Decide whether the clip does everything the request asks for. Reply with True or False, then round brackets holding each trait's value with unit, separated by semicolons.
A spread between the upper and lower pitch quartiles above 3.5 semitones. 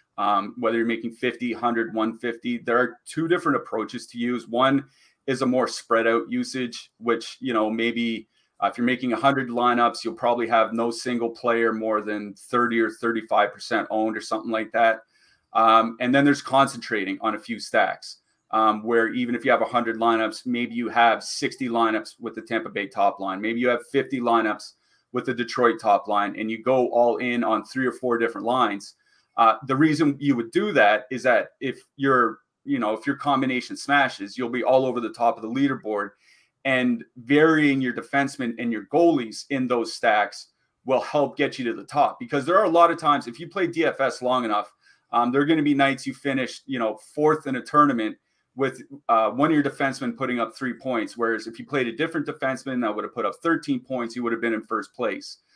False (2.8 semitones)